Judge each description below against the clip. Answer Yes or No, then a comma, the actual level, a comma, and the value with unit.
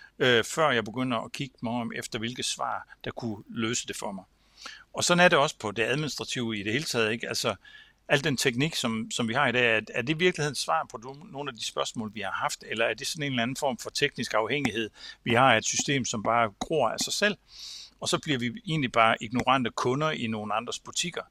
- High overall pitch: No, low, 125 Hz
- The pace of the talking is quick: Yes, fast, 240 wpm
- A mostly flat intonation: No, average, 4.2 semitones